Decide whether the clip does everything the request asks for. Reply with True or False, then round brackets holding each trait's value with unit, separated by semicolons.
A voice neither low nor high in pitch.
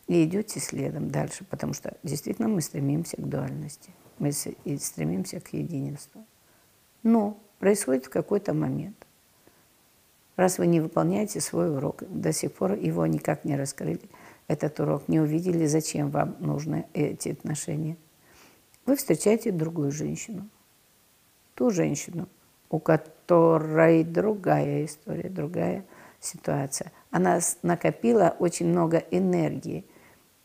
True (165 Hz)